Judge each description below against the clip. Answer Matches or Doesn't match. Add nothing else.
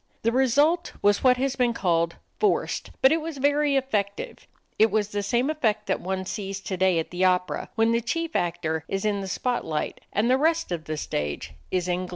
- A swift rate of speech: Matches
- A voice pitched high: Matches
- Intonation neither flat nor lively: Doesn't match